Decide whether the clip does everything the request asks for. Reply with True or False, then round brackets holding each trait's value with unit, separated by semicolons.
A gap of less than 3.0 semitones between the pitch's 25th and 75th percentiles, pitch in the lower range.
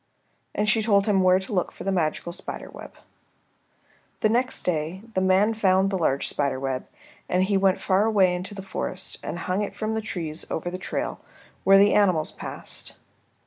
False (2.5 semitones; 190 Hz)